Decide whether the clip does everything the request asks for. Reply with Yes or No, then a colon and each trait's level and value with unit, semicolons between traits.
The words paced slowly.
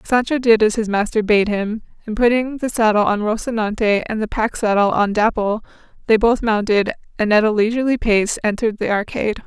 No: average, 190 wpm